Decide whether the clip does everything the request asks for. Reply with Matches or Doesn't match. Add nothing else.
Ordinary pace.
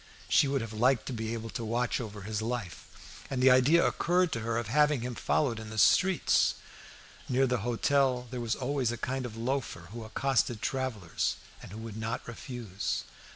Matches